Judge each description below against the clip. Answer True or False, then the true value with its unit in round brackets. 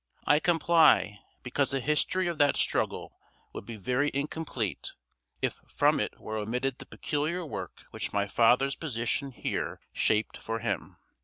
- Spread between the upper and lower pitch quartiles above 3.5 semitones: True (4.9 semitones)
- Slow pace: False (150 wpm)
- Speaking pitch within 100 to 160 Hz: True (135 Hz)